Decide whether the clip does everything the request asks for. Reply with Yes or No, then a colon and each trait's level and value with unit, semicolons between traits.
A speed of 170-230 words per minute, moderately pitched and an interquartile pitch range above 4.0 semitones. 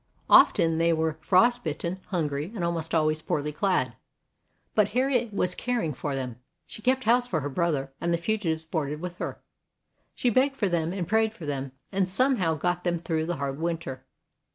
Yes: average, 190 wpm; medium, 170 Hz; average, 4.8 semitones